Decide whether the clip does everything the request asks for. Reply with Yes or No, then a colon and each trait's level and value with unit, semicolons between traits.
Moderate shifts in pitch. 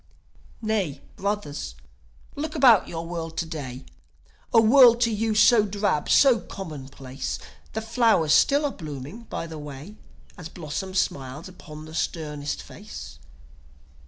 No: wide, 6.7 semitones